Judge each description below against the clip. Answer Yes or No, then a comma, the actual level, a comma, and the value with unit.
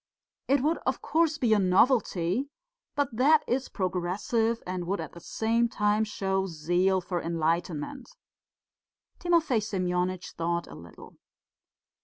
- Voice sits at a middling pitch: No, high, 195 Hz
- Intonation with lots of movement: Yes, wide, 5.7 semitones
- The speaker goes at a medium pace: No, slow, 130 wpm